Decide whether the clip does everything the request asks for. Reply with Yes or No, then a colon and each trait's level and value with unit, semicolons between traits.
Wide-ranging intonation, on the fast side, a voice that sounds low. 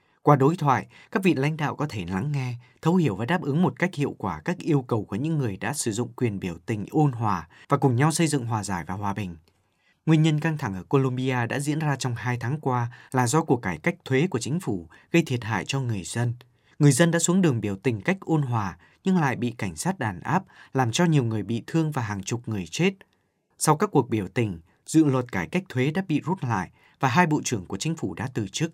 Yes: wide, 5.7 semitones; fast, 260 wpm; low, 130 Hz